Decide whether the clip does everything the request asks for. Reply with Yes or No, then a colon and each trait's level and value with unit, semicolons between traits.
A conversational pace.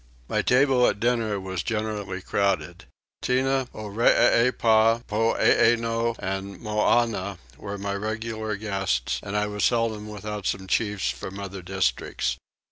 No: slow, 125 wpm